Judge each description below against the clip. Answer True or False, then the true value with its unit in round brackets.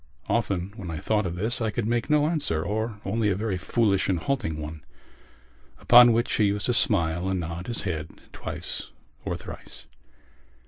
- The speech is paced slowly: False (180 wpm)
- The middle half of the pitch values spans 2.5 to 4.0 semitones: False (4.9 semitones)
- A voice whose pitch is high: False (100 Hz)